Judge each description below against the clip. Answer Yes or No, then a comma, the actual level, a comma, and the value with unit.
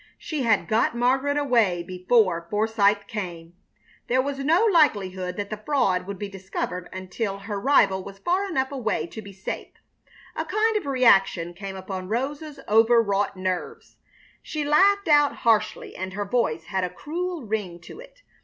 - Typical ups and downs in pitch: No, wide, 6.8 semitones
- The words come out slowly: No, average, 165 wpm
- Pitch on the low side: No, high, 215 Hz